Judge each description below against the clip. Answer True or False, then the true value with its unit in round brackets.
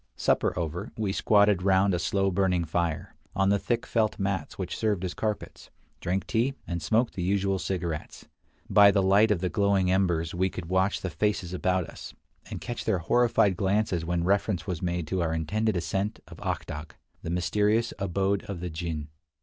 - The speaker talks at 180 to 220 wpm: True (190 wpm)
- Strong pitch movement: False (2.7 semitones)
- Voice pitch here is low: True (95 Hz)